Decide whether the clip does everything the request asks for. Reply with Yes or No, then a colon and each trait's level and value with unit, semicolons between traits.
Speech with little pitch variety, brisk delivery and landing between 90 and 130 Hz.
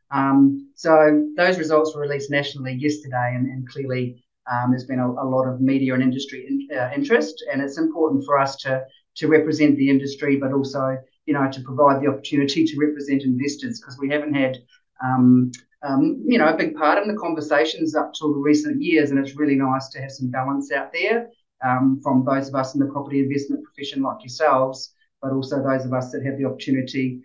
No: narrow, 2.2 semitones; fast, 210 wpm; medium, 140 Hz